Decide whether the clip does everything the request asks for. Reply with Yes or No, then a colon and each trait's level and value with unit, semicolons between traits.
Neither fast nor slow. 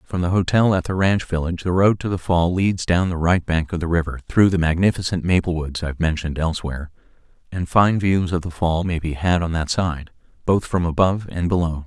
No: fast, 235 wpm